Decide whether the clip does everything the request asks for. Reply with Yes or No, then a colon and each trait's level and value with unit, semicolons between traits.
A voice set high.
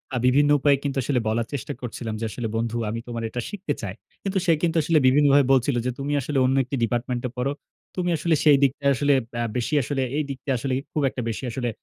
No: low, 135 Hz